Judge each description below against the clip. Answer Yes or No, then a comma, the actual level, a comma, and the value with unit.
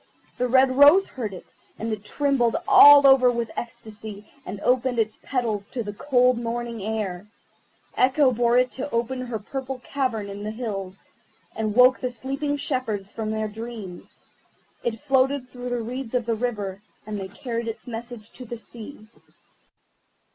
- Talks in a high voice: Yes, high, 235 Hz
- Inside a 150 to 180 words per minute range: Yes, average, 160 wpm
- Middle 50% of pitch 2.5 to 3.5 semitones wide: Yes, average, 2.9 semitones